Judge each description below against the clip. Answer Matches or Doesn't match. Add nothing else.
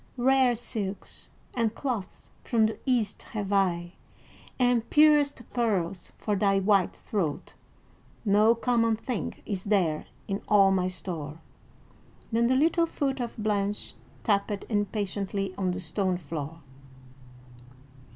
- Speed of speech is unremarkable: Doesn't match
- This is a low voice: Doesn't match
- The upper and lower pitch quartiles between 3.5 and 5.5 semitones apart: Matches